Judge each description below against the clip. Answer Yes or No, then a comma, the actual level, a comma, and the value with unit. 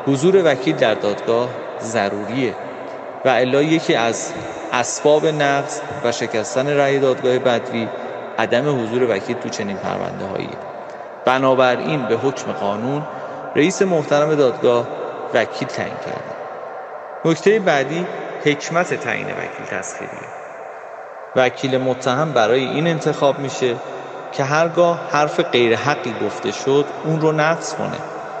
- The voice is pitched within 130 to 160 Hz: Yes, medium, 140 Hz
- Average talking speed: Yes, average, 120 wpm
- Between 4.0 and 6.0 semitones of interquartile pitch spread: No, average, 3.3 semitones